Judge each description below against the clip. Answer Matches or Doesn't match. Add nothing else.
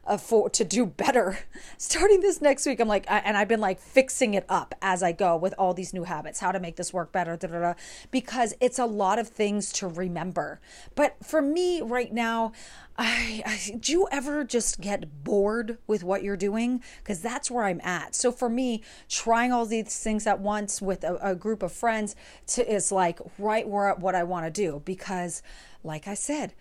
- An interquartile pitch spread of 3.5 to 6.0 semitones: Matches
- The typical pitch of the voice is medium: Doesn't match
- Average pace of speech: Doesn't match